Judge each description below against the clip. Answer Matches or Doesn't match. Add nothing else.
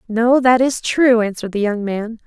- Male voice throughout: Doesn't match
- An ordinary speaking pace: Doesn't match